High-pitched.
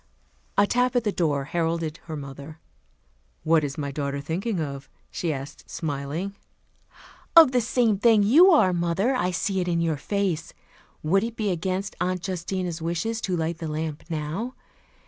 No: medium, 175 Hz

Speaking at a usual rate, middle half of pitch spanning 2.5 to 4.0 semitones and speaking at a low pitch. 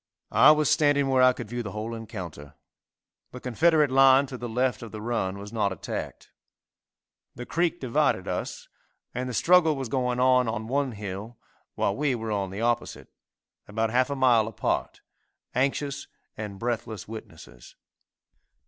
Yes: average, 160 wpm; average, 3.6 semitones; low, 120 Hz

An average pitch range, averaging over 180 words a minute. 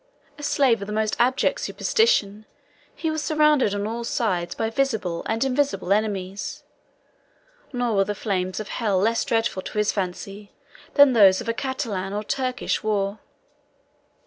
No: average, 4.3 semitones; average, 155 wpm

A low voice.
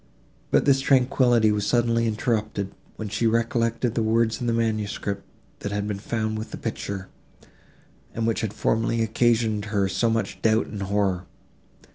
Yes: low, 110 Hz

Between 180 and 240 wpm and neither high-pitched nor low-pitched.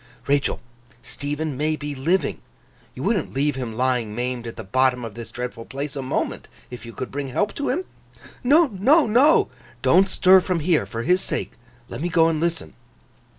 Yes: average, 190 wpm; medium, 145 Hz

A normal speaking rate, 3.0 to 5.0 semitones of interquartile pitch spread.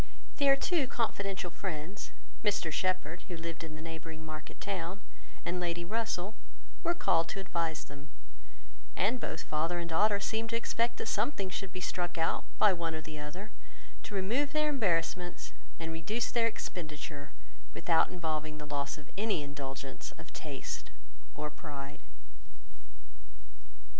Yes: average, 150 wpm; average, 4.6 semitones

